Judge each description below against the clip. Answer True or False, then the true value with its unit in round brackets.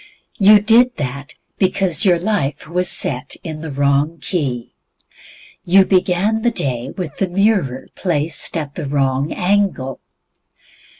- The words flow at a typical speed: False (130 wpm)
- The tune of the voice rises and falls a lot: True (5.7 semitones)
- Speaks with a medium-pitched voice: True (170 Hz)